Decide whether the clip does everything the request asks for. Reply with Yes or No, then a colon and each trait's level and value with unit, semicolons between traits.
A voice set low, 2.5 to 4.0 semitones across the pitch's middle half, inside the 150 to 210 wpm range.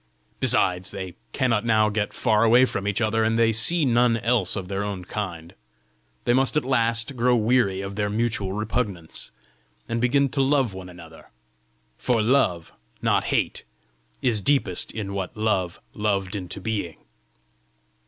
Yes: low, 110 Hz; average, 3.7 semitones; average, 155 wpm